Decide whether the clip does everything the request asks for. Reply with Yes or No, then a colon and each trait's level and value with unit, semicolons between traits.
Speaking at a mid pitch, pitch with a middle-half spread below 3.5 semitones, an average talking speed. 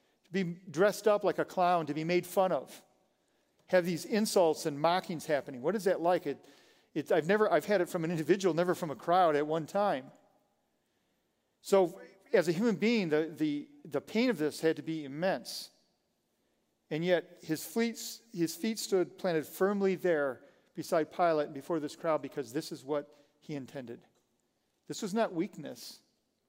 No: medium, 175 Hz; average, 3.8 semitones; average, 180 wpm